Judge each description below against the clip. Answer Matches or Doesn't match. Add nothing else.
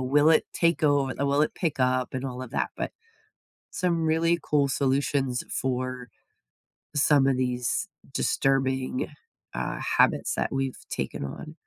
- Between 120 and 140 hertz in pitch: Matches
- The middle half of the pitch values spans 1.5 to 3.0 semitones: Matches